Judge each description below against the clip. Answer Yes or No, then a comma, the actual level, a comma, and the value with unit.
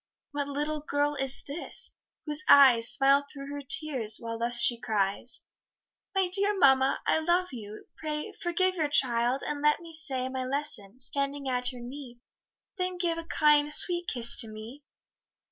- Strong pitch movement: No, average, 3.8 semitones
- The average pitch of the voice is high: Yes, very high, 280 Hz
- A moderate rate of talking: Yes, average, 165 wpm